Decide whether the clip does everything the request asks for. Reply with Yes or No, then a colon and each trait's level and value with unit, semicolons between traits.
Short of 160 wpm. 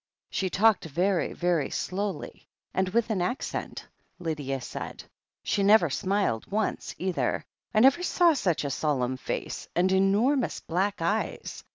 Yes: average, 145 wpm